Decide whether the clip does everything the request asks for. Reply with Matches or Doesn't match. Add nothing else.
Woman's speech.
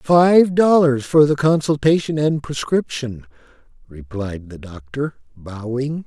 Doesn't match